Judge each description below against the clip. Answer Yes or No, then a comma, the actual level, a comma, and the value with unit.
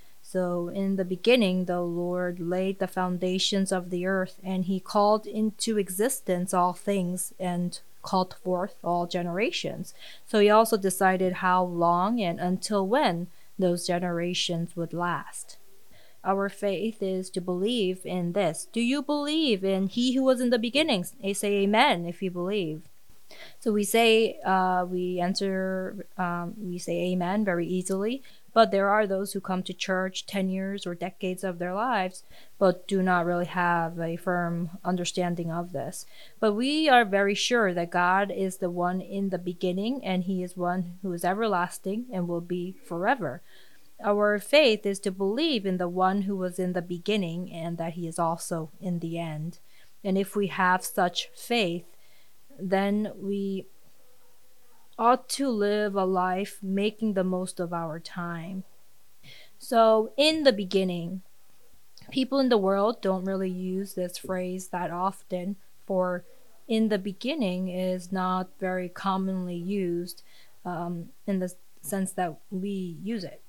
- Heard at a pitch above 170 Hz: Yes, medium, 185 Hz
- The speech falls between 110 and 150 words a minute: No, average, 160 wpm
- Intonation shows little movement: Yes, narrow, 2.3 semitones